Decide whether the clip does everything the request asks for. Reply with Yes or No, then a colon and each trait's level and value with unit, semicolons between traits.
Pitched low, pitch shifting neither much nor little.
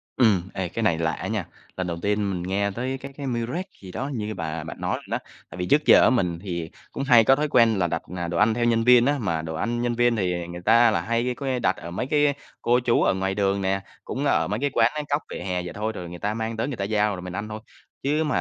Yes: low, 110 Hz; average, 5.0 semitones